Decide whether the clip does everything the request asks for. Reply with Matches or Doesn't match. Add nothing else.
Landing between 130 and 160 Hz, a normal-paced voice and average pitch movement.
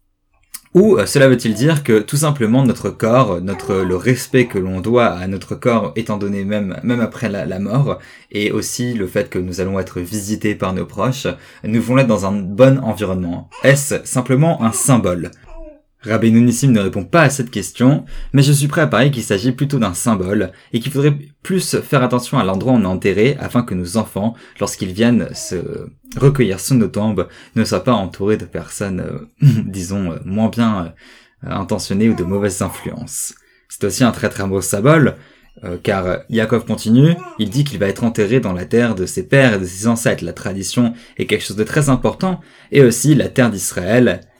Doesn't match